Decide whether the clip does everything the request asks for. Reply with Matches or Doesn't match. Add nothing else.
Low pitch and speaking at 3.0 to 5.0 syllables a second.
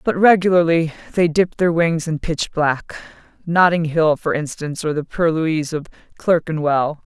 Doesn't match